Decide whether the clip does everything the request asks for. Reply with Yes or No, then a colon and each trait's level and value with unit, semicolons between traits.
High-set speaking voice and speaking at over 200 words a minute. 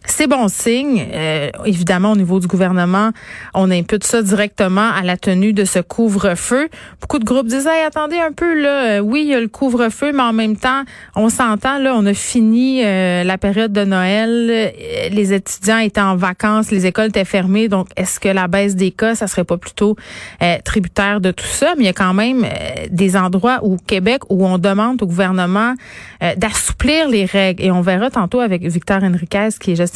Yes: high, 210 Hz; average, 210 wpm